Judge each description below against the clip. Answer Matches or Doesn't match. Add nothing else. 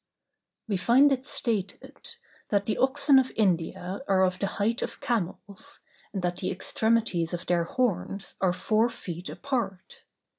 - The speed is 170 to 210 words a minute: Doesn't match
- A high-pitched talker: Matches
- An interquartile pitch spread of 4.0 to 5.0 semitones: Matches